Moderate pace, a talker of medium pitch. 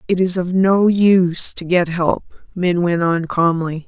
Yes: average, 185 wpm; medium, 175 Hz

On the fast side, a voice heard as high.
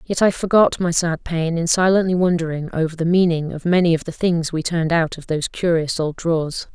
No: fast, 220 wpm; medium, 165 Hz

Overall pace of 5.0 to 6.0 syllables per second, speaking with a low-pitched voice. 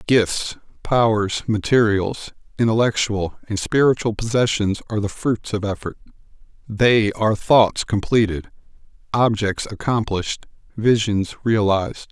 No: 4.5 syllables/s; low, 110 Hz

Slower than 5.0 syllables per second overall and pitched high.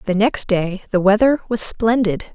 Yes: 4.7 syllables/s; high, 210 Hz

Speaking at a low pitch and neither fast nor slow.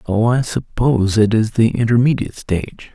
Yes: low, 115 Hz; average, 165 wpm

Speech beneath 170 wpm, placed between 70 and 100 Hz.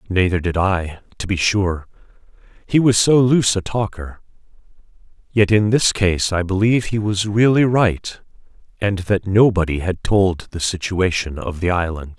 Yes: average, 160 wpm; very low, 95 Hz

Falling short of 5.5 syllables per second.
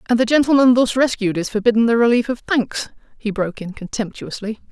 No: 6.0 syllables/s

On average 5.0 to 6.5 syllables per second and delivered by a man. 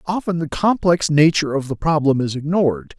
Yes: 5.6 syllables/s; male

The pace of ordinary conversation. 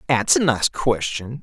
Yes: average, 170 wpm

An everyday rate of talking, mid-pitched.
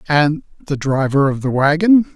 Yes: average, 165 wpm; medium, 150 Hz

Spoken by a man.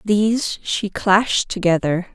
No: female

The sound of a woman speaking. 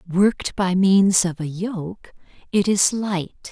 Yes: female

